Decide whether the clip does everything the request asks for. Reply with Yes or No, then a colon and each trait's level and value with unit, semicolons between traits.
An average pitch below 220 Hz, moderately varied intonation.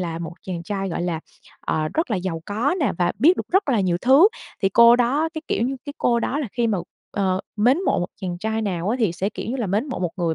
No: high, 210 Hz; wide, 5.7 semitones